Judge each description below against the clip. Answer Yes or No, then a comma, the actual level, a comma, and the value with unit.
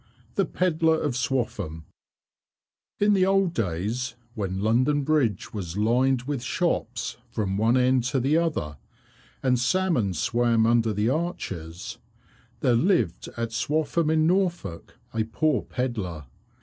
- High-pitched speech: No, low, 125 Hz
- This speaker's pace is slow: Yes, slow, 130 wpm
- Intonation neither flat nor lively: No, wide, 6.8 semitones